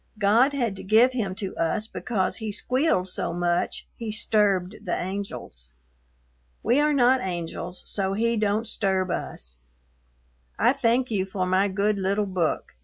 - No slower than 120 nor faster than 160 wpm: Yes, average, 155 wpm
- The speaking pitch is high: Yes, high, 200 Hz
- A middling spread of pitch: Yes, average, 3.7 semitones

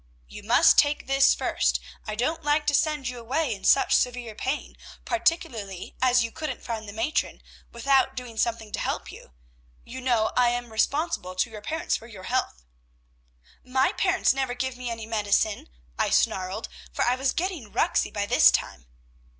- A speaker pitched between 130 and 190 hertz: No, high, 245 Hz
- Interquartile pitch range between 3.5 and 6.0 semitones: Yes, average, 3.8 semitones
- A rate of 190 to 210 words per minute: No, average, 175 wpm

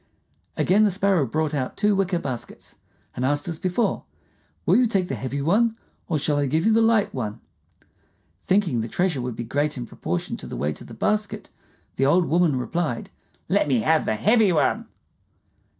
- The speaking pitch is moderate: Yes, medium, 160 Hz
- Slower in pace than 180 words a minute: No, average, 190 wpm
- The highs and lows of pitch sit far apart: Yes, wide, 7.1 semitones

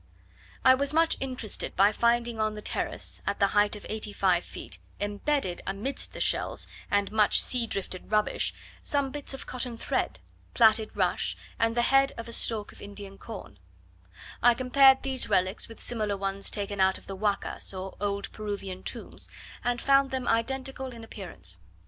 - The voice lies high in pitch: Yes, high, 215 Hz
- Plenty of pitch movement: No, average, 4.2 semitones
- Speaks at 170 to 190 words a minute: Yes, average, 175 wpm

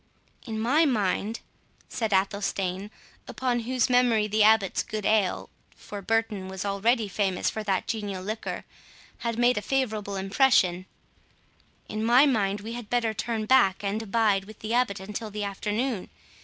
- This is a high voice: Yes, high, 215 Hz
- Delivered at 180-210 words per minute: No, average, 150 wpm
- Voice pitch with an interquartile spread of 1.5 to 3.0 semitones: Yes, average, 2.7 semitones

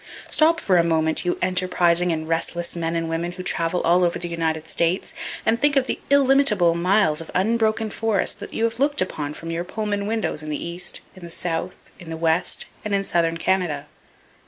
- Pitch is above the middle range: No, medium, 175 Hz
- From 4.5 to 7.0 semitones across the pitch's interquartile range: No, average, 4.0 semitones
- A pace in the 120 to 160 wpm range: No, fast, 205 wpm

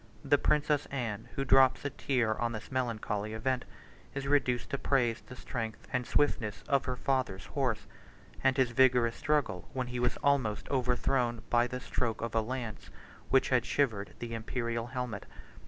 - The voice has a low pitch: Yes, low, 125 Hz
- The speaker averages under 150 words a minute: No, average, 170 wpm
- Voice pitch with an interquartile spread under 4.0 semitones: Yes, narrow, 2.6 semitones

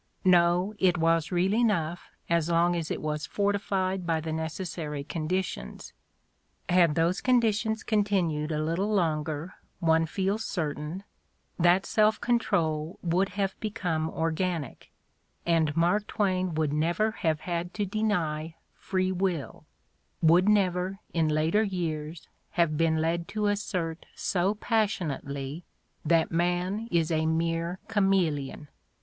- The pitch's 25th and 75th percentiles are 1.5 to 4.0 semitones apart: Yes, average, 3.4 semitones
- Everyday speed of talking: No, slow, 130 wpm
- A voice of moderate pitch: Yes, medium, 175 Hz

